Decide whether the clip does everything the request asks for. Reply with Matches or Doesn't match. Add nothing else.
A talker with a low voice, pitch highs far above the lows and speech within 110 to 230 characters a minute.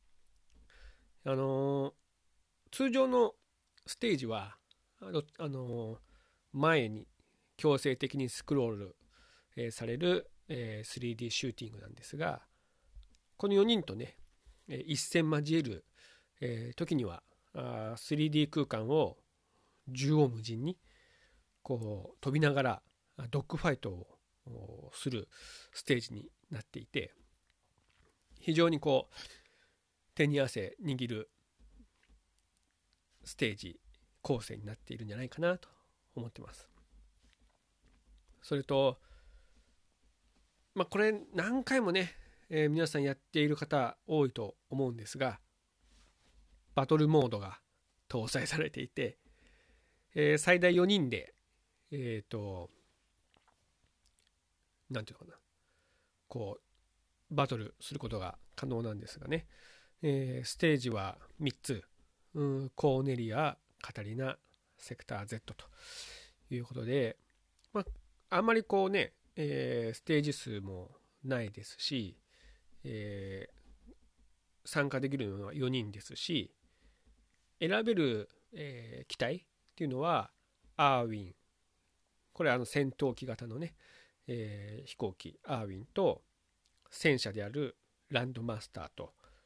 Matches